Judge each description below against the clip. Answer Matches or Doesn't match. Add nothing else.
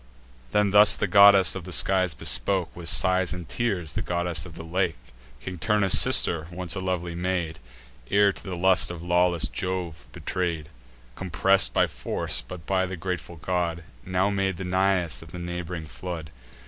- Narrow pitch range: Matches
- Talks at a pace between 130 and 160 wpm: Doesn't match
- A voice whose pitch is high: Doesn't match